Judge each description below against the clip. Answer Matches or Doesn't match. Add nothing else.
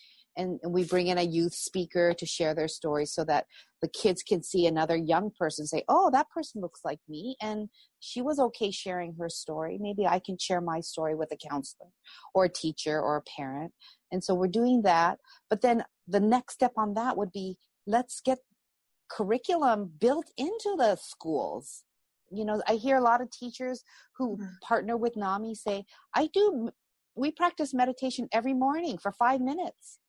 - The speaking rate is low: Doesn't match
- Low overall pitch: Doesn't match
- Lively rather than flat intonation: Matches